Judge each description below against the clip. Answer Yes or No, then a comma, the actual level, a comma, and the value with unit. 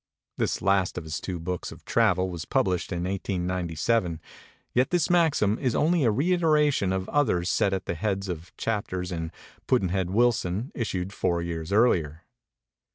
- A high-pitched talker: No, very low, 95 Hz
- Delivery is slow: No, average, 160 wpm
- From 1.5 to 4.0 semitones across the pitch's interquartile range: No, average, 5.0 semitones